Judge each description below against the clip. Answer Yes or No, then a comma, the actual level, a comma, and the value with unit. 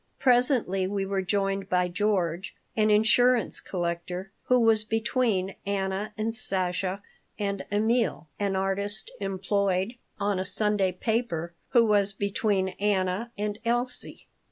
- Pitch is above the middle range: Yes, high, 200 Hz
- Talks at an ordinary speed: No, slow, 125 wpm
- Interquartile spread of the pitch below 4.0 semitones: Yes, narrow, 2.6 semitones